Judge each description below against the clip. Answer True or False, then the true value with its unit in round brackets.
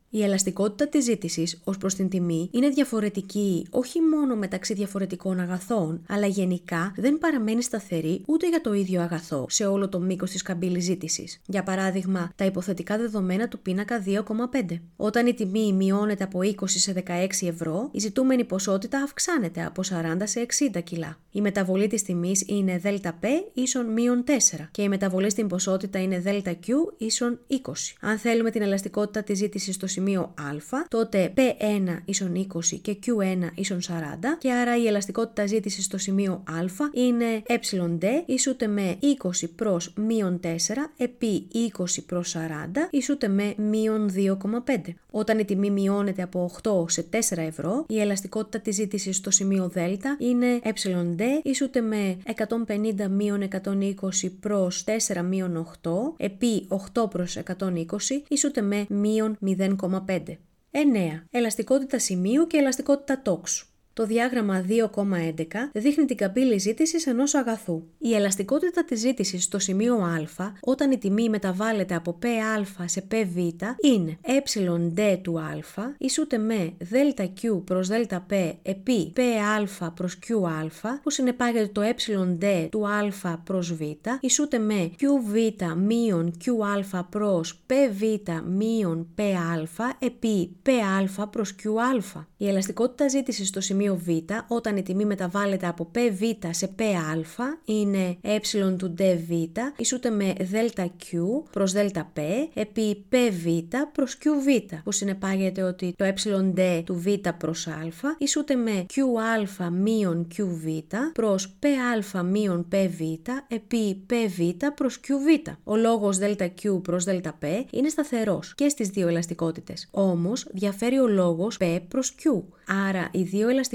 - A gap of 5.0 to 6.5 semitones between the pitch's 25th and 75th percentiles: False (4.3 semitones)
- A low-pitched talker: False (200 Hz)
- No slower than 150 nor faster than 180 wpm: False (140 wpm)